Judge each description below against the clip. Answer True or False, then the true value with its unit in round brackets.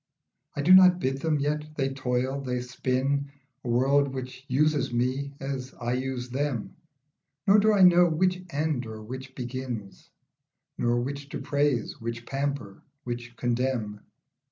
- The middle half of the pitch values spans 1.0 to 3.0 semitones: True (2.6 semitones)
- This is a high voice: False (135 Hz)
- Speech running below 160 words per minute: True (150 wpm)